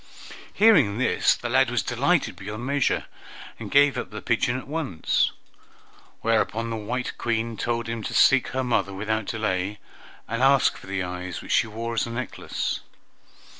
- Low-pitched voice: Yes, low, 115 Hz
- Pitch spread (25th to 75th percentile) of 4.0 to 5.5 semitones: No, average, 3.5 semitones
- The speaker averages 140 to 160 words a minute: No, average, 170 wpm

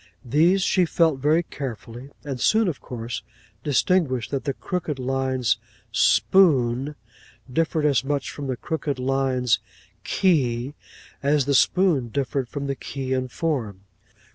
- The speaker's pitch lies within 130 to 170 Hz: Yes, medium, 140 Hz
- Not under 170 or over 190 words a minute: No, slow, 135 wpm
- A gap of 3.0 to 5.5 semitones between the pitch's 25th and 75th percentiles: Yes, average, 3.4 semitones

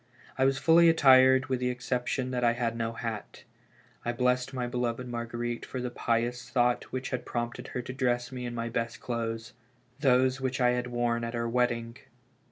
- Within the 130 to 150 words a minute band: No, average, 195 wpm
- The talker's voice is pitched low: Yes, low, 125 Hz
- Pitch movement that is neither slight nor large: No, narrow, 1.4 semitones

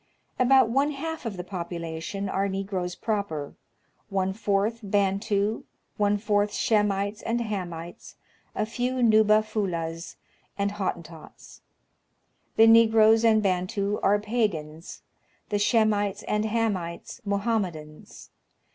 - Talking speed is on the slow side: Yes, slow, 110 wpm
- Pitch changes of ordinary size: Yes, average, 3.0 semitones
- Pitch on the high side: Yes, high, 205 Hz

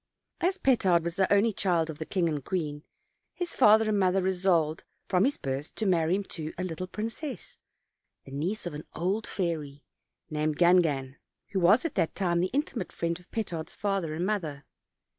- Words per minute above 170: Yes, average, 185 wpm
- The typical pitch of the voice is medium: Yes, medium, 180 Hz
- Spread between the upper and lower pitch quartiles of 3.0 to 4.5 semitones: Yes, average, 4.2 semitones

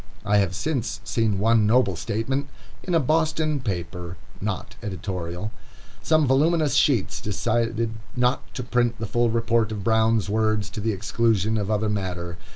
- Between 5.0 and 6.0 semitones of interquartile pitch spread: No, average, 3.4 semitones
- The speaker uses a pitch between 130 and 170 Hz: No, low, 110 Hz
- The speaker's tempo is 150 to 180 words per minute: Yes, average, 155 wpm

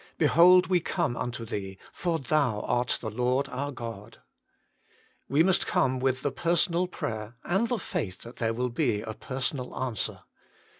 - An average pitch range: No, wide, 6.4 semitones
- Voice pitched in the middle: No, low, 130 Hz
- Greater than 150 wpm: Yes, average, 160 wpm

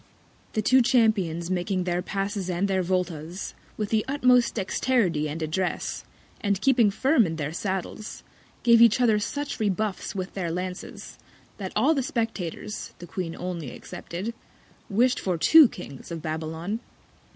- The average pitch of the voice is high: Yes, high, 195 Hz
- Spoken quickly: No, average, 150 wpm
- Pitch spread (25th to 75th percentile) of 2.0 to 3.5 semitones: No, average, 4.6 semitones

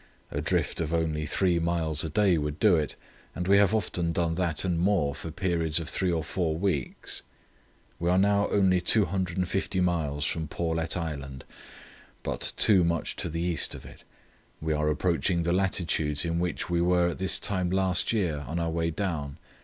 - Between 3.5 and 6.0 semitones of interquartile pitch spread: No, narrow, 2.5 semitones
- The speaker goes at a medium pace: Yes, average, 185 wpm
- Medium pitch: No, very low, 85 Hz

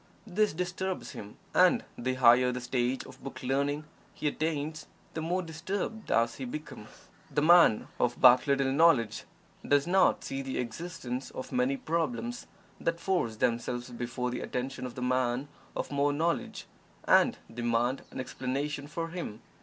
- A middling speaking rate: Yes, average, 155 wpm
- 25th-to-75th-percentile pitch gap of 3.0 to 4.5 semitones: No, average, 5.1 semitones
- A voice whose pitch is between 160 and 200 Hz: No, low, 135 Hz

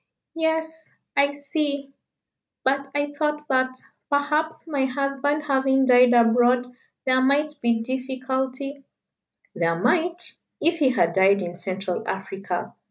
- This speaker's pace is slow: Yes, slow, 125 wpm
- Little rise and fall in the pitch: No, average, 3.0 semitones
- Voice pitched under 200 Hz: No, very high, 270 Hz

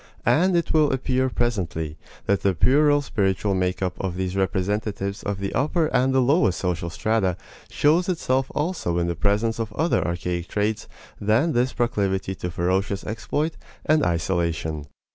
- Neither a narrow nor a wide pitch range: No, wide, 6.3 semitones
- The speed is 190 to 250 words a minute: No, average, 160 wpm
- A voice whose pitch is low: Yes, low, 105 Hz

